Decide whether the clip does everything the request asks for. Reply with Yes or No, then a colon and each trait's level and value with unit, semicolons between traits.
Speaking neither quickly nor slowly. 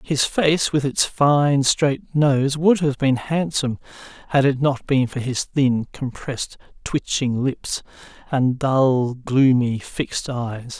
Yes: average, 145 wpm